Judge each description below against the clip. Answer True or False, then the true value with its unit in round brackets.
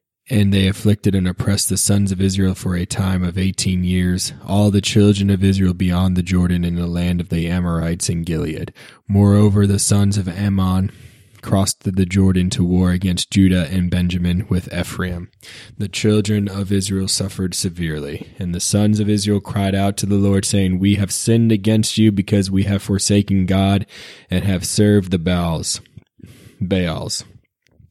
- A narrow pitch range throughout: True (2.0 semitones)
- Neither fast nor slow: True (170 wpm)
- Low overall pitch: True (95 Hz)